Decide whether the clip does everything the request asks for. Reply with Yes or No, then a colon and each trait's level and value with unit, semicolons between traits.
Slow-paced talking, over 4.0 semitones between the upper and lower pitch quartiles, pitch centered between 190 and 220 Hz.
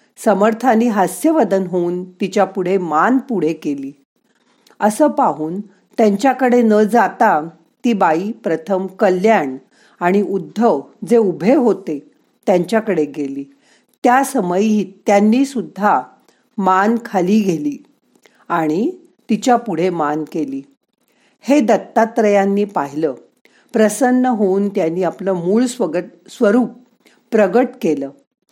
No: average, 100 wpm; average, 4.9 semitones; high, 205 Hz